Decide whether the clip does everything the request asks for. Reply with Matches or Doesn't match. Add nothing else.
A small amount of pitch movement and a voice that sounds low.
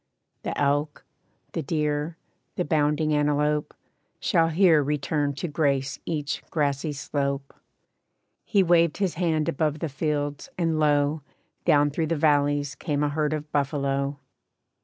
Doesn't match